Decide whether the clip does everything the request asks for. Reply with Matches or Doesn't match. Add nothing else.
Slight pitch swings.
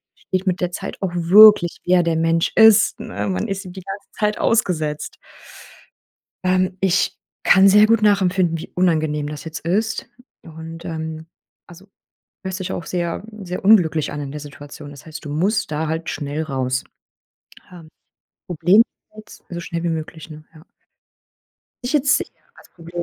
Doesn't match